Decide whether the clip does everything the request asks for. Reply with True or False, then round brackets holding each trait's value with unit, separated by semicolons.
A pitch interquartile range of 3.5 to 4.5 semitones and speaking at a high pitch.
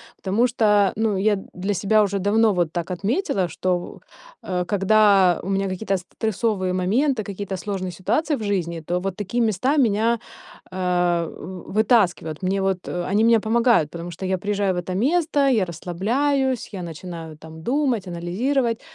True (3.8 semitones; 195 Hz)